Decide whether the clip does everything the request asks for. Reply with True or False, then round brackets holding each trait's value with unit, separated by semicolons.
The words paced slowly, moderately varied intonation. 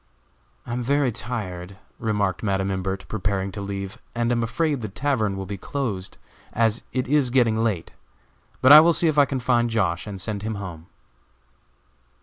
False (175 wpm; 4.3 semitones)